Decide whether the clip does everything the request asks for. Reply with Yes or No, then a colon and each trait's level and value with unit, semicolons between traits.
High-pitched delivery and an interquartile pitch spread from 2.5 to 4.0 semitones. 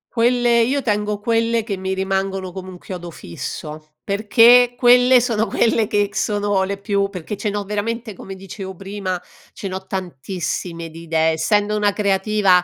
Yes: high, 200 Hz; average, 2.8 semitones